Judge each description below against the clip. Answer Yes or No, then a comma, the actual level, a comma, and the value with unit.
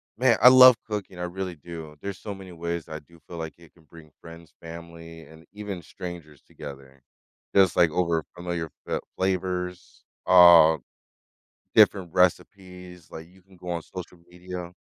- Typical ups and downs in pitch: No, narrow, 2.0 semitones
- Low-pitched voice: Yes, very low, 85 Hz